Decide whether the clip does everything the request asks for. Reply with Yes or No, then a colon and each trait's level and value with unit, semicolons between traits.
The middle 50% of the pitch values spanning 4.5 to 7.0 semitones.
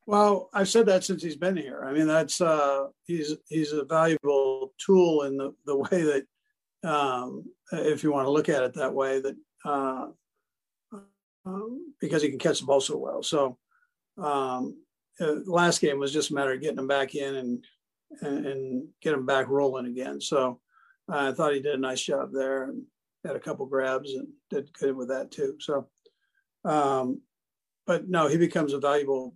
Yes: average, 5.2 semitones